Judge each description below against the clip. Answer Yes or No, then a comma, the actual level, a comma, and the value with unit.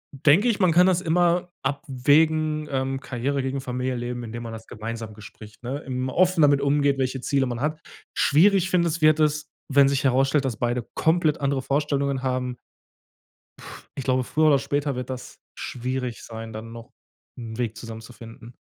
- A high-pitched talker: No, low, 135 Hz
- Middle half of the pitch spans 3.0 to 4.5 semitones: Yes, average, 3.8 semitones